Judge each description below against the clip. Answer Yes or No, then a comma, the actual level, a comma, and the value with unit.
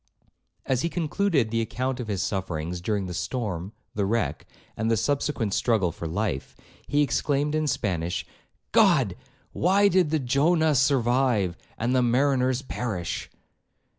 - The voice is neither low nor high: No, low, 125 Hz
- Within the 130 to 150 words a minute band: Yes, average, 140 wpm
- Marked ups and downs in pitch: Yes, wide, 6.0 semitones